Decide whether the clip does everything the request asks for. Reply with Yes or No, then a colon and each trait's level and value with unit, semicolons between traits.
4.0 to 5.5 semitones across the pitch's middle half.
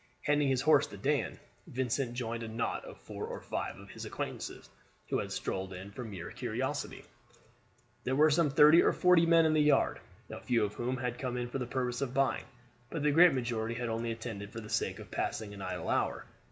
Yes: average, 4.4 semitones